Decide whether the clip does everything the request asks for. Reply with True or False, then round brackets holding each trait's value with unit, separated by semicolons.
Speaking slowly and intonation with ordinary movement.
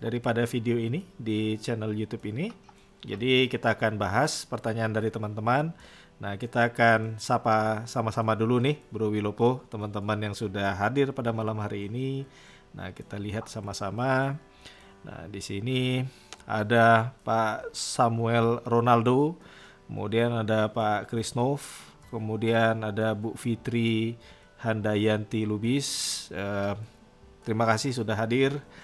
False (120 wpm; 2.2 semitones)